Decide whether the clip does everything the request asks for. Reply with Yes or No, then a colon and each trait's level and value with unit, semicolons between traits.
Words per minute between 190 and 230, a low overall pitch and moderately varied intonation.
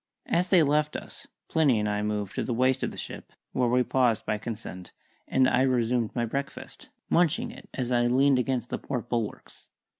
Yes: average, 200 wpm; low, 125 Hz; average, 3.2 semitones